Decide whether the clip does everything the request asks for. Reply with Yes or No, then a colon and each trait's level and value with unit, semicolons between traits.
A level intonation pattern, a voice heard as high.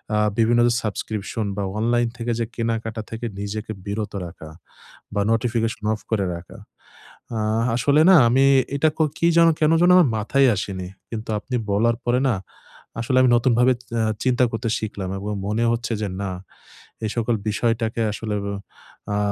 No: narrow, 2.2 semitones; low, 115 Hz